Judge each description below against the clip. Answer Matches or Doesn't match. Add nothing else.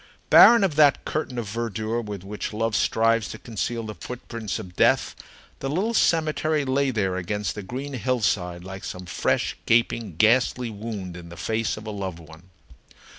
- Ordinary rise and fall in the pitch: Matches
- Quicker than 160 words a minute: Matches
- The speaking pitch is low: Matches